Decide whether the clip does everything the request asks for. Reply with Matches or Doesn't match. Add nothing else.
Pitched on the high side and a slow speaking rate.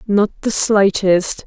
Matches